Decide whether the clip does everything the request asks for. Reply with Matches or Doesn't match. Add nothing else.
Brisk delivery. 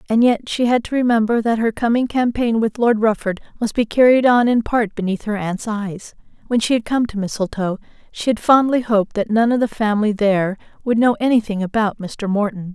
Matches